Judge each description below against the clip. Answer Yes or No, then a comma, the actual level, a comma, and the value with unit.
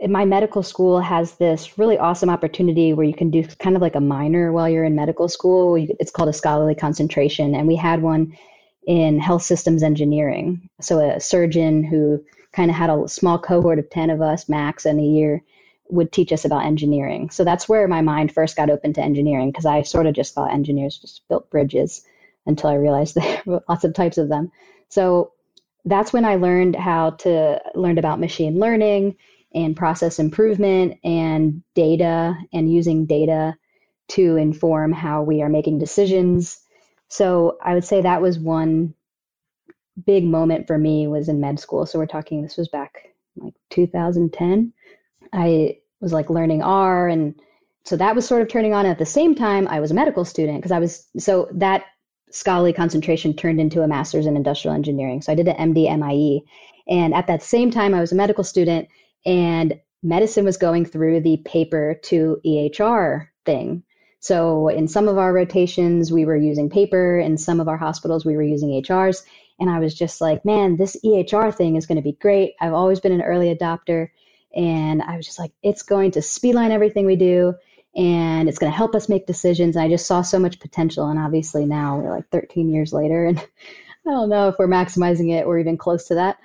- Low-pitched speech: No, medium, 170 Hz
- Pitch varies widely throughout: No, average, 2.9 semitones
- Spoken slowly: No, average, 200 wpm